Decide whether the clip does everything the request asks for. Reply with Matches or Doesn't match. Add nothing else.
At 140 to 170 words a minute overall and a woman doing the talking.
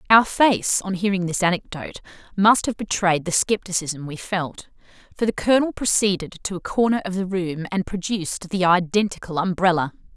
Matches